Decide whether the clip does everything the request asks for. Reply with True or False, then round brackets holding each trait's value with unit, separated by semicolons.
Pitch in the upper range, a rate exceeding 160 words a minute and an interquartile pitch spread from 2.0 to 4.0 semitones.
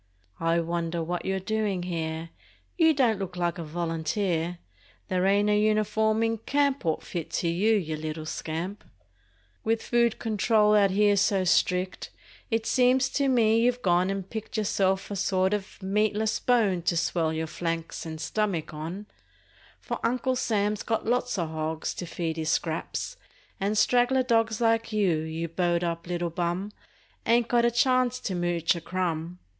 False (195 Hz; 170 wpm; 4.6 semitones)